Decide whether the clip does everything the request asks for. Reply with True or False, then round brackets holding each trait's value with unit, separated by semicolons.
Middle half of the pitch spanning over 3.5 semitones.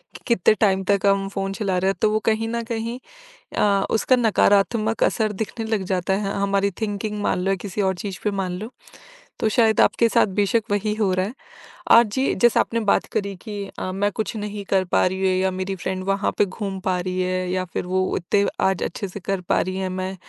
False (2.4 semitones)